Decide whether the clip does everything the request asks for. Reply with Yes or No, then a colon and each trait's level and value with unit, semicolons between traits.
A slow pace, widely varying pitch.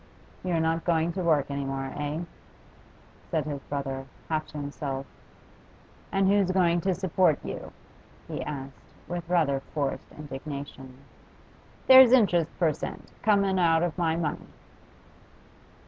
No: slow, 130 wpm; average, 4.0 semitones